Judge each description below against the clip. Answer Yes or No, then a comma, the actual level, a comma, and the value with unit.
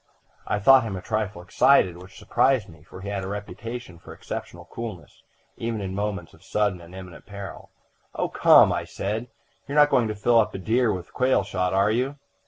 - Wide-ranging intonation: No, average, 3.8 semitones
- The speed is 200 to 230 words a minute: Yes, fast, 205 wpm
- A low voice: Yes, low, 105 Hz